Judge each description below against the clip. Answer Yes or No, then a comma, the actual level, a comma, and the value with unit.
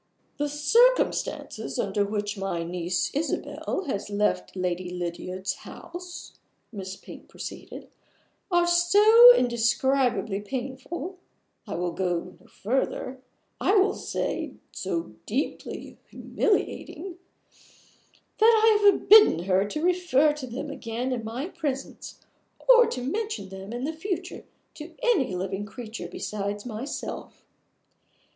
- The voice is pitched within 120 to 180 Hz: No, very high, 255 Hz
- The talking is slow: Yes, slow, 115 wpm